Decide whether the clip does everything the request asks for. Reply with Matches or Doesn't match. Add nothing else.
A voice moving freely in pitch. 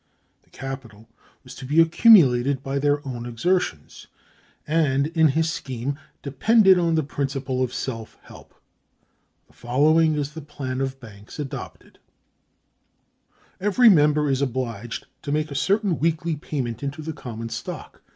Doesn't match